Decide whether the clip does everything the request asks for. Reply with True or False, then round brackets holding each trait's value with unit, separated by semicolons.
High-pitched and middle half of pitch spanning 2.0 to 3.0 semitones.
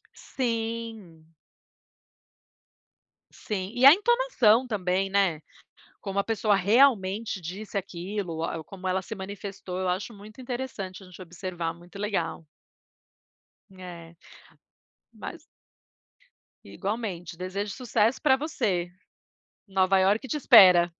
False (195 Hz; 3.7 semitones)